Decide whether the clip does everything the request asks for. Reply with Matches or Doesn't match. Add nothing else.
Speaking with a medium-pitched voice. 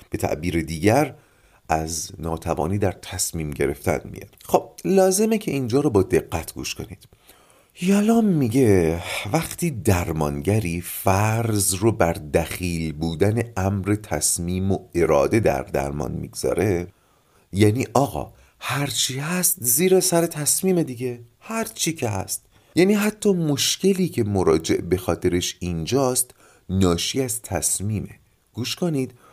Doesn't match